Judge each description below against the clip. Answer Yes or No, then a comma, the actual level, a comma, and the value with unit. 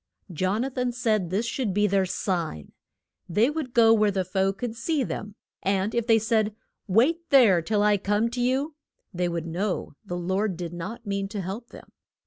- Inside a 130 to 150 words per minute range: No, average, 195 wpm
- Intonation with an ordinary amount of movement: Yes, average, 3.9 semitones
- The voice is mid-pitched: No, high, 210 Hz